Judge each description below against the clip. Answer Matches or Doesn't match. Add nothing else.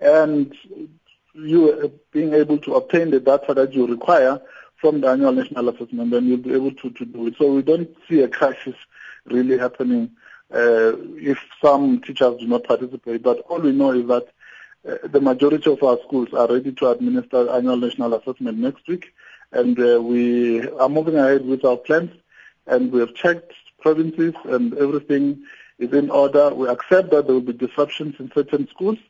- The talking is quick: Doesn't match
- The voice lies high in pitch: Doesn't match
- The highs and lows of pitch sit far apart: Doesn't match